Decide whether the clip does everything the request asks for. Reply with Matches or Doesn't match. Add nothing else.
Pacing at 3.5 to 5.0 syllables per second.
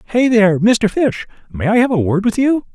Doesn't match